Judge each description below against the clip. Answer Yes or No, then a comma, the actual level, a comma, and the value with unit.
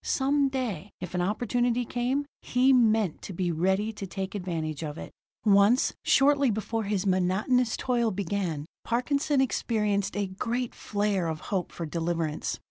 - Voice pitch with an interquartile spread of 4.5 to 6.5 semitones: Yes, average, 5.2 semitones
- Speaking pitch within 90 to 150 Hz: No, high, 205 Hz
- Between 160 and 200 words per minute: No, average, 150 wpm